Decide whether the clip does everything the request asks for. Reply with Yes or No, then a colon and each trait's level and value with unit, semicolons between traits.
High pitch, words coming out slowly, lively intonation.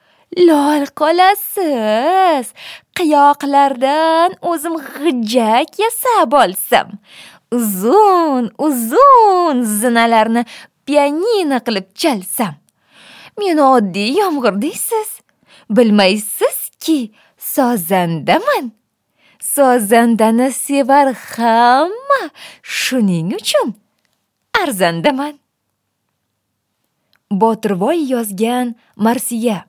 Yes: very high, 260 Hz; slow, 55 wpm; wide, 6.1 semitones